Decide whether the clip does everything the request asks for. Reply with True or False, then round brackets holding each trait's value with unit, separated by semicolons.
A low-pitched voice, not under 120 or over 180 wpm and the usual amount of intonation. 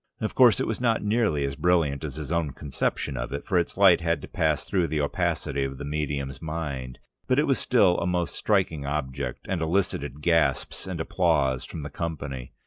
False (80 Hz; 205 wpm; 4.2 semitones)